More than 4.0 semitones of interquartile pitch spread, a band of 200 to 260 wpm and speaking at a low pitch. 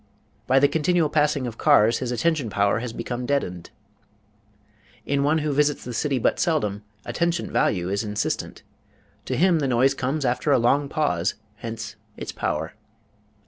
No: average, 4.6 semitones; average, 160 wpm; low, 130 Hz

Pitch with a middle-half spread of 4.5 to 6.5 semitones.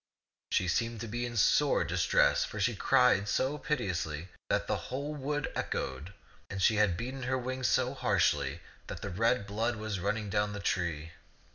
Yes: average, 5.1 semitones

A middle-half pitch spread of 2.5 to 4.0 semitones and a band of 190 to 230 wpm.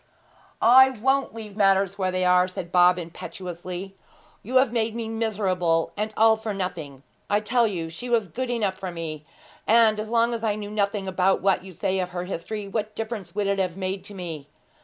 Yes: average, 3.4 semitones; average, 200 wpm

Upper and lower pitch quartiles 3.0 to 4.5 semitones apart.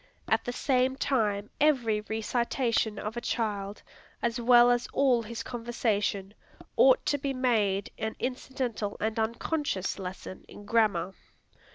Yes: average, 3.3 semitones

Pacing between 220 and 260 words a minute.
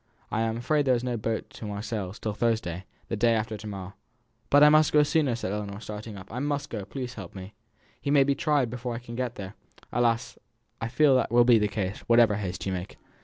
Yes: fast, 235 wpm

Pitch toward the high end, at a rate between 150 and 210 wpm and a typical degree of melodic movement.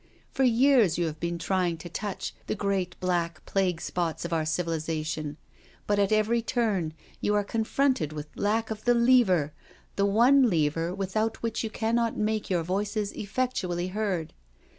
Yes: high, 195 Hz; average, 160 wpm; average, 4.6 semitones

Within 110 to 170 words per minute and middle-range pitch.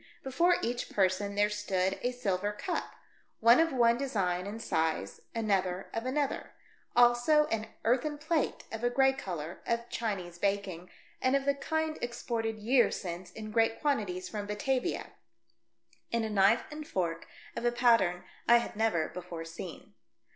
No: average, 160 wpm; high, 225 Hz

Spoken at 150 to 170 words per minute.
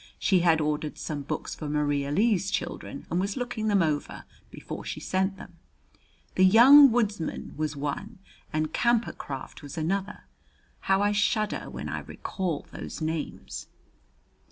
Yes: average, 155 wpm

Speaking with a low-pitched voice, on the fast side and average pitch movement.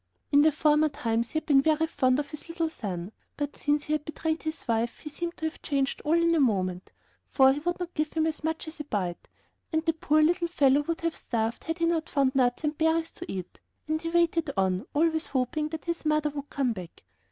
No: very high, 305 Hz; fast, 240 wpm; average, 3.3 semitones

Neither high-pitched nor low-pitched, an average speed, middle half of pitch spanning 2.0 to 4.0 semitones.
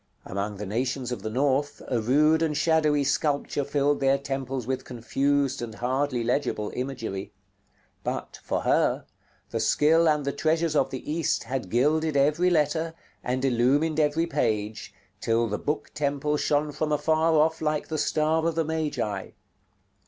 Yes: medium, 145 Hz; average, 160 wpm; average, 3.6 semitones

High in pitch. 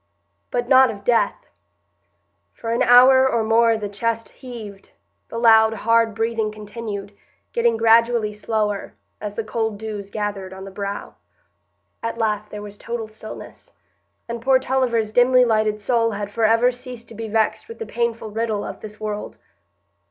Yes: high, 225 Hz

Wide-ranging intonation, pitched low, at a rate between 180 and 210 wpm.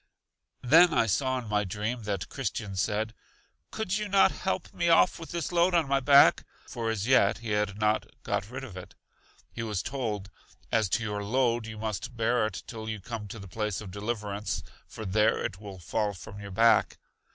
No: average, 3.7 semitones; low, 110 Hz; average, 200 wpm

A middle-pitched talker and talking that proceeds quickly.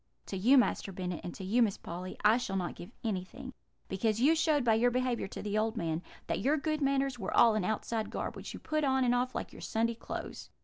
No: high, 230 Hz; fast, 245 wpm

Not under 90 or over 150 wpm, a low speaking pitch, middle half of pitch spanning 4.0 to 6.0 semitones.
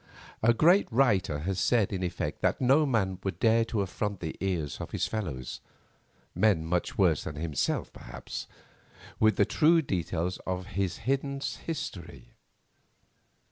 Yes: average, 140 wpm; very low, 95 Hz; average, 5.1 semitones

